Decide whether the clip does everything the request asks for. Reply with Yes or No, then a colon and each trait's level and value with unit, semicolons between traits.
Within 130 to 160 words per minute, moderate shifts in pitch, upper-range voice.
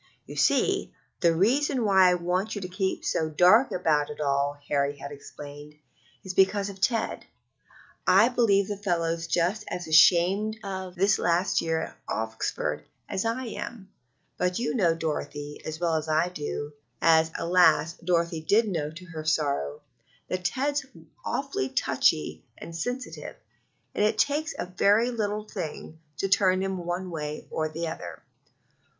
No: average, 155 wpm; average, 4.3 semitones; medium, 180 Hz